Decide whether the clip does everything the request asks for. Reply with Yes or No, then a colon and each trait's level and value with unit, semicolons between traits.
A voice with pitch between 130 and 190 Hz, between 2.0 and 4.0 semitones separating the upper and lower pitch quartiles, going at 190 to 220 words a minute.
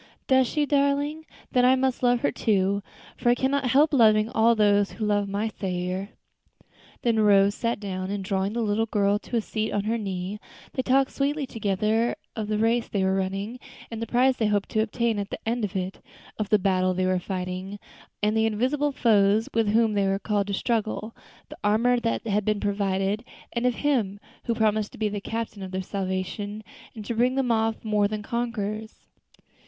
No: high, 215 Hz; average, 2.8 semitones; average, 200 wpm